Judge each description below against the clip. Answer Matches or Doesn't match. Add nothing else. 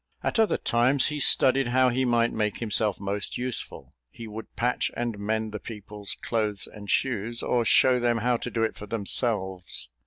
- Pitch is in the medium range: Doesn't match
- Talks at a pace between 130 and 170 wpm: Doesn't match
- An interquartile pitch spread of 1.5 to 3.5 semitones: Matches